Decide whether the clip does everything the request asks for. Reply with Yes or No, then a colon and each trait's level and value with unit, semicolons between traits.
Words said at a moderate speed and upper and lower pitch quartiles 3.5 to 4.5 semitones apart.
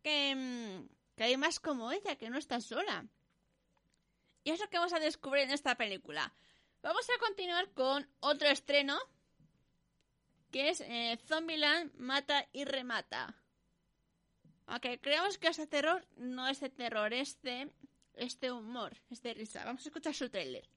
Yes: average, 160 wpm; average, 4.1 semitones